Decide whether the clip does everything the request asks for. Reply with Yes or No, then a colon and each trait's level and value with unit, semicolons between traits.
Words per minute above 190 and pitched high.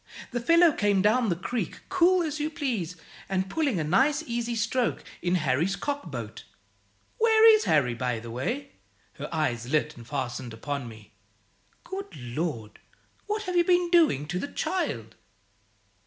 No: average, 155 wpm; high, 195 Hz